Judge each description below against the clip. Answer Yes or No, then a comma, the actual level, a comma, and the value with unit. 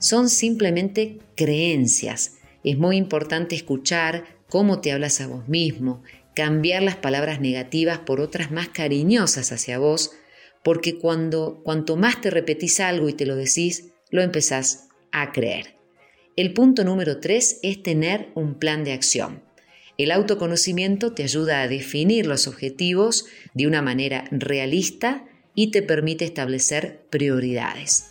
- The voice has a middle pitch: Yes, medium, 160 Hz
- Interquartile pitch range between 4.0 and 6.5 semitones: Yes, average, 4.7 semitones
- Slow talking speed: No, average, 140 wpm